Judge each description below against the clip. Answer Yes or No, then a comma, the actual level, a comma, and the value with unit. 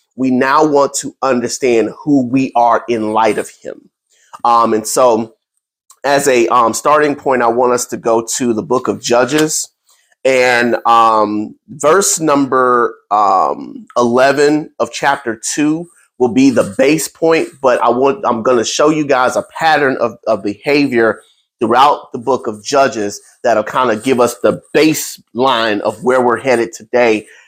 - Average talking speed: Yes, average, 160 wpm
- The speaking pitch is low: Yes, low, 125 Hz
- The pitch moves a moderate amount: Yes, average, 4.0 semitones